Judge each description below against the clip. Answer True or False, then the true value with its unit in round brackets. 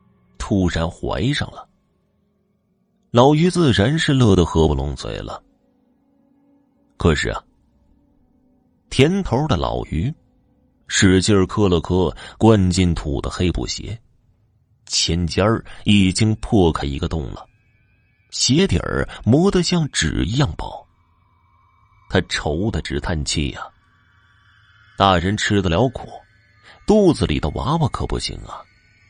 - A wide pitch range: False (4.7 semitones)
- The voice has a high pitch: False (100 Hz)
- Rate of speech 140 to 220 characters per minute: True (165 characters per minute)